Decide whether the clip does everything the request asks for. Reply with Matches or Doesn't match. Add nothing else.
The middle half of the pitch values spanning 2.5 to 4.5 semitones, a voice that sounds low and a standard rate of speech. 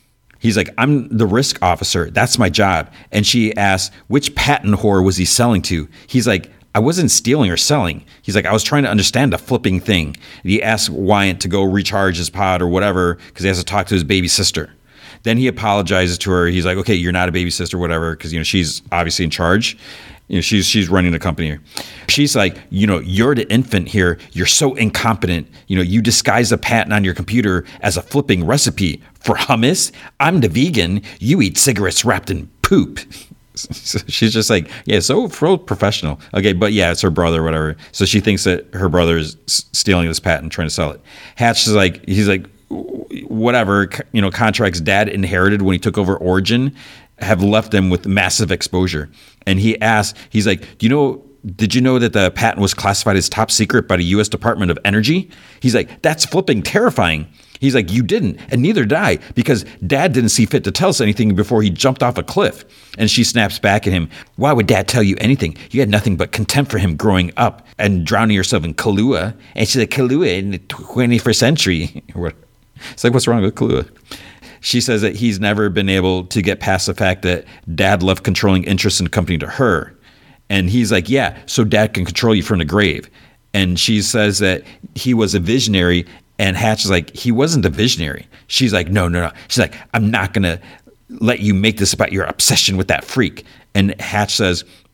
Doesn't match